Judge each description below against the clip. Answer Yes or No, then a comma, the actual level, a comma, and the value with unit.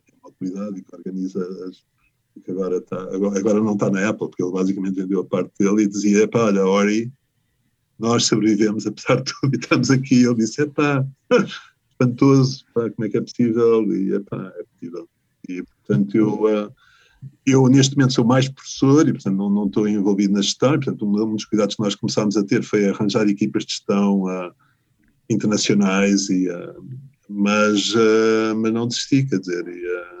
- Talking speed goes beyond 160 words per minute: Yes, average, 180 wpm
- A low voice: Yes, low, 110 Hz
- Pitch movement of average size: Yes, average, 4.1 semitones